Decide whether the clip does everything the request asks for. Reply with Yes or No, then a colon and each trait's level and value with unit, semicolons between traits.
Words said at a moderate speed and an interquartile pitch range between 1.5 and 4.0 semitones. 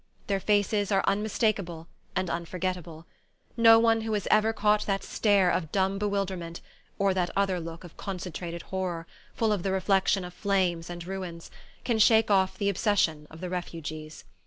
Yes: average, 165 wpm; average, 2.9 semitones